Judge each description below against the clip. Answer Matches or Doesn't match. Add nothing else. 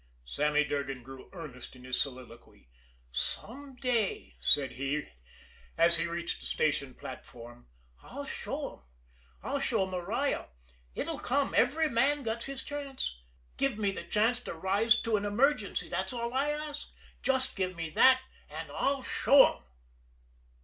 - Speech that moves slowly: Doesn't match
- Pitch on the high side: Matches